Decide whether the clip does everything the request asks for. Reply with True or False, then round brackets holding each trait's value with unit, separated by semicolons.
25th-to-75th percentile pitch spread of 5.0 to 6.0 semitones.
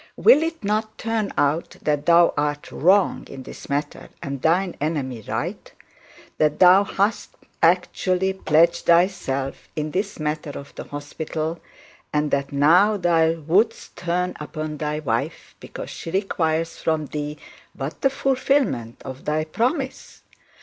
False (4.4 semitones)